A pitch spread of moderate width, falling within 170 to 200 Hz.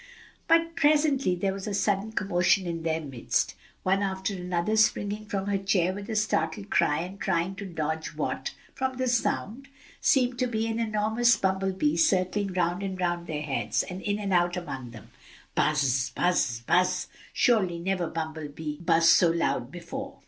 Yes: average, 4.1 semitones; high, 190 Hz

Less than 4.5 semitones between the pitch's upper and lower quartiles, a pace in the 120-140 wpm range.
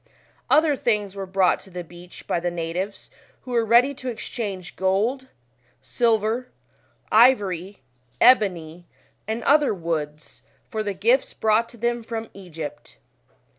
No: average, 4.9 semitones; slow, 135 wpm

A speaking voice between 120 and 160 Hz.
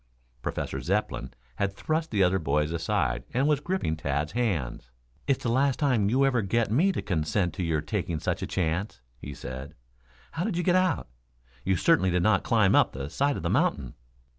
No: very low, 95 Hz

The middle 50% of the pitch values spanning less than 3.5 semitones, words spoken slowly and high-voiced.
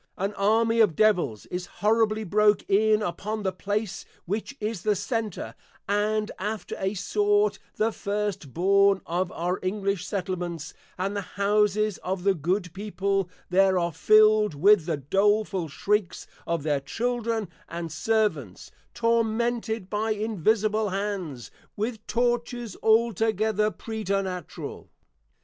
Yes: average, 2.9 semitones; slow, 125 wpm; high, 205 Hz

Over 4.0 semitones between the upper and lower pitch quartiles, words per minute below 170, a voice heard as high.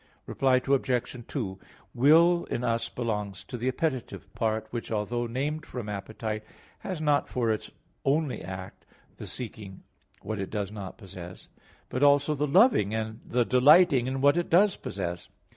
No: average, 5.2 semitones; average, 160 wpm; low, 120 Hz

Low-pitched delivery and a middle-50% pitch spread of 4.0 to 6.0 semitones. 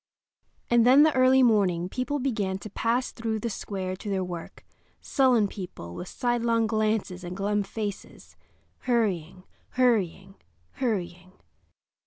No: high, 215 Hz; average, 4.4 semitones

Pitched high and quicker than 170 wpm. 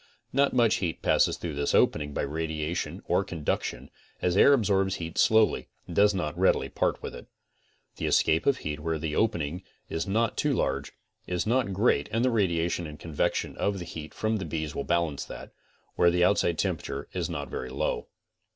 No: very low, 85 Hz; average, 190 wpm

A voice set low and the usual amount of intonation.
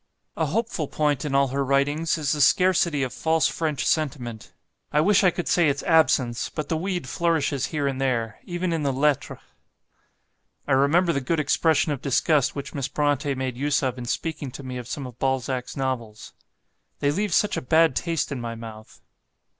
No: medium, 145 Hz; average, 3.5 semitones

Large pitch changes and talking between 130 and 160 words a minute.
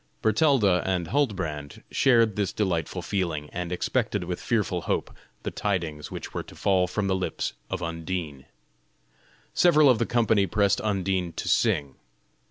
No: average, 3.9 semitones; average, 150 wpm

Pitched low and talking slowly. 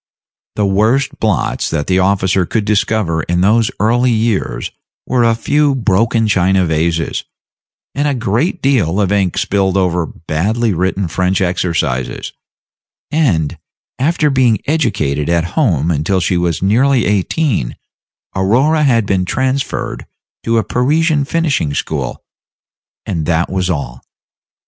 Yes: low, 100 Hz; slow, 130 wpm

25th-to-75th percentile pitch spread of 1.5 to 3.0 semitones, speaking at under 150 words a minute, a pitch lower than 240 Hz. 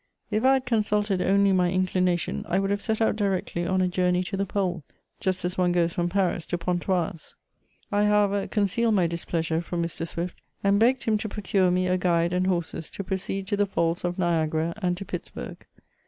No: narrow, 2.4 semitones; fast, 205 wpm; medium, 185 Hz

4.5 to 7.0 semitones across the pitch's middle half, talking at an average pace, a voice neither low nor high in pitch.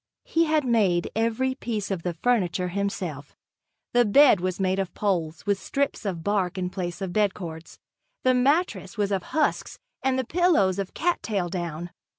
No: wide, 5.5 semitones; average, 170 wpm; high, 200 Hz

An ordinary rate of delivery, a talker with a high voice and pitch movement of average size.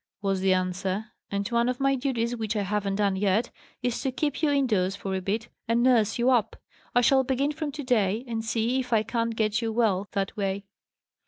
No: fast, 220 wpm; high, 225 Hz; average, 3.8 semitones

